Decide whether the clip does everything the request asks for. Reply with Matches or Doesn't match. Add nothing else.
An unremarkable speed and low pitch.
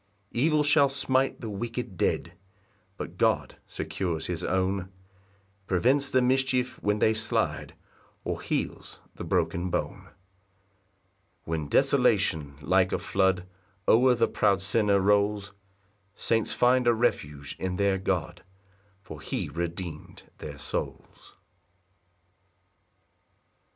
Doesn't match